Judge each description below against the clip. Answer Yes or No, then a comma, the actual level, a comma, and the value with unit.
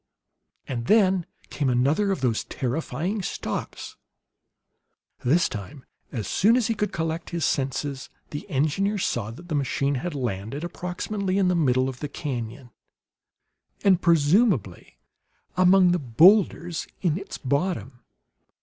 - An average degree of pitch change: No, wide, 6.2 semitones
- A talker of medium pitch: Yes, medium, 155 Hz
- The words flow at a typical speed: No, slow, 130 wpm